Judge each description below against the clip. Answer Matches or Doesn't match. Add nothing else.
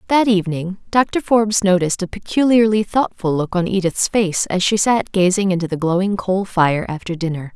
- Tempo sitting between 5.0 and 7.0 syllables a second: Matches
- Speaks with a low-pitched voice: Doesn't match